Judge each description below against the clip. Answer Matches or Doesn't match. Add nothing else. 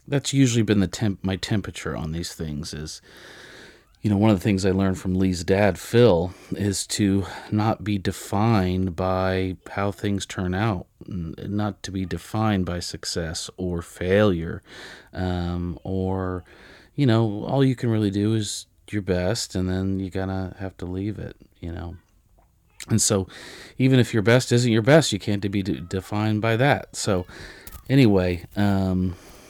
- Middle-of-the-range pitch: Doesn't match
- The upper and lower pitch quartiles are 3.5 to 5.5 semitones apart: Doesn't match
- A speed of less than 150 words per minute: Doesn't match